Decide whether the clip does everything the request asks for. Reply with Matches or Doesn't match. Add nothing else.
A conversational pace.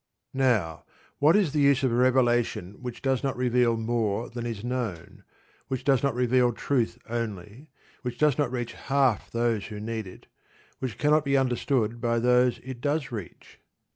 Matches